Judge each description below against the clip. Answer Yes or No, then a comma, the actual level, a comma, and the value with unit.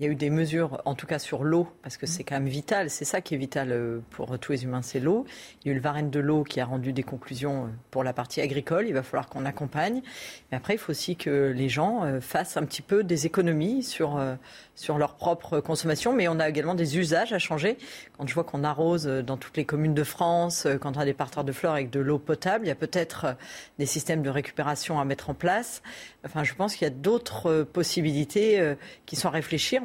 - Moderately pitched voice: Yes, medium, 150 Hz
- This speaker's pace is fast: Yes, fast, 245 wpm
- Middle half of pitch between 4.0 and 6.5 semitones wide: No, average, 3.6 semitones